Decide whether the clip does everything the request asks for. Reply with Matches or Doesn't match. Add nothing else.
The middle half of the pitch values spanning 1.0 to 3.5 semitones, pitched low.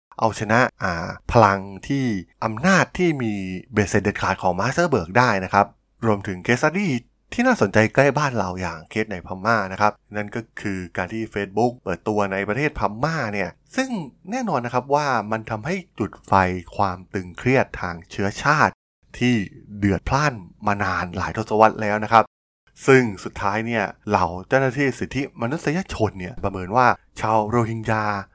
Doesn't match